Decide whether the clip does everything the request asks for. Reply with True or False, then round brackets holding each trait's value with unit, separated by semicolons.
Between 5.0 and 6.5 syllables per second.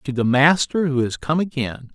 False (4.8 syllables/s)